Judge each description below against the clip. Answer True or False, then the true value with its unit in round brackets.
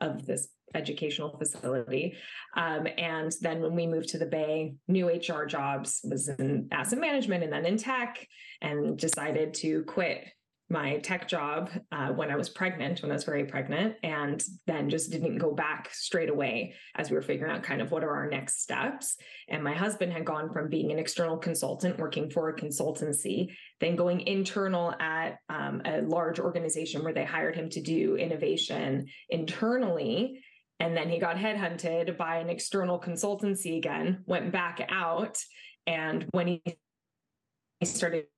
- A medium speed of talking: True (170 wpm)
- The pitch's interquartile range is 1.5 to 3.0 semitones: True (2.7 semitones)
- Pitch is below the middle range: False (165 Hz)